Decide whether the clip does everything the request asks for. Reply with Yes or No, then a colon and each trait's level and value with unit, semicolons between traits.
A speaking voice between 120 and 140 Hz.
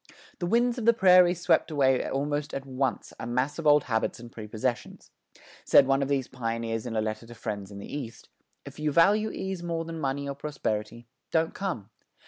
Yes: low, 135 Hz